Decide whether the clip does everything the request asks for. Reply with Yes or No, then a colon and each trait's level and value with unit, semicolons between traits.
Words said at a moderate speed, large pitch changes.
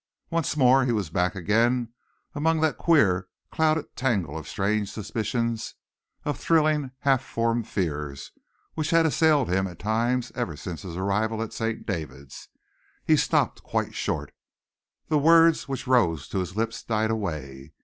Yes: average, 150 wpm; wide, 6.7 semitones